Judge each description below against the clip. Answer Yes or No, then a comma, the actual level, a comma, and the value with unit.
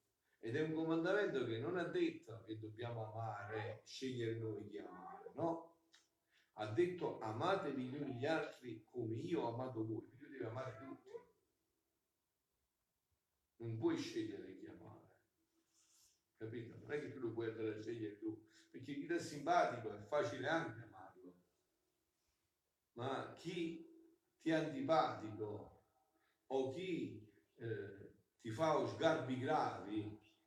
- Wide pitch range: Yes, wide, 8.7 semitones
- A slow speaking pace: No, average, 130 wpm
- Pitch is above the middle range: No, medium, 145 Hz